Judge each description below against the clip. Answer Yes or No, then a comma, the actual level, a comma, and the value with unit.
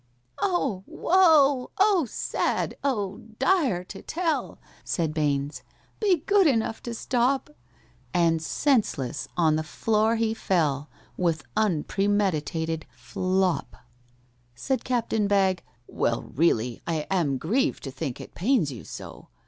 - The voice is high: Yes, high, 195 Hz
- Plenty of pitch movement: Yes, wide, 8.6 semitones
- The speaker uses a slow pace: Yes, slow, 120 wpm